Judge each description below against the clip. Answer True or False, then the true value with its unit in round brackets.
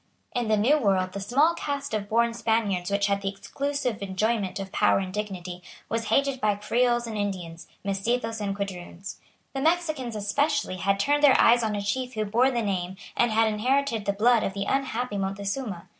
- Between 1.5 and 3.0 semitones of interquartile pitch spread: False (3.9 semitones)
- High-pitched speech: True (215 Hz)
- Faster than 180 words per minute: True (190 wpm)